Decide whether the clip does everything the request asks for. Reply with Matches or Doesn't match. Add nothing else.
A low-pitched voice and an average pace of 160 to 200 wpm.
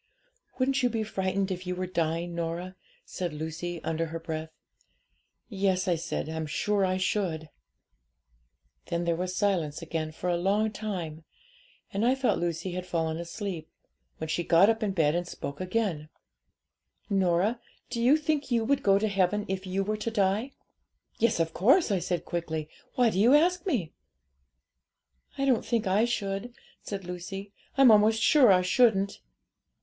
Doesn't match